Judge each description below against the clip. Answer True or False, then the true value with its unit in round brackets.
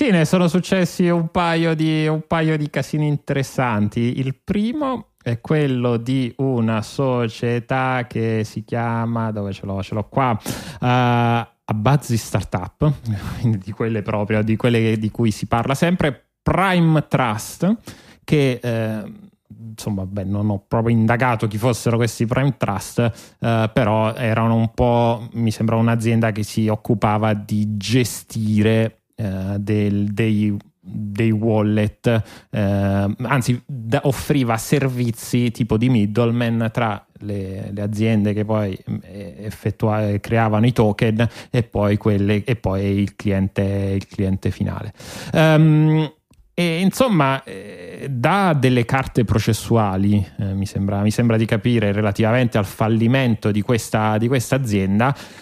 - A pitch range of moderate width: True (3.6 semitones)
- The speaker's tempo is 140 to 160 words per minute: False (130 wpm)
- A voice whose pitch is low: True (115 Hz)